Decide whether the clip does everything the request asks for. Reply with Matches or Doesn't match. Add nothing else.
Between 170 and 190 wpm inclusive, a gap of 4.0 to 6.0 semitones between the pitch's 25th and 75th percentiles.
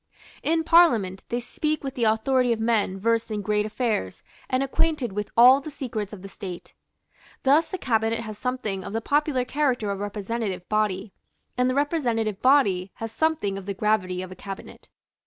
Matches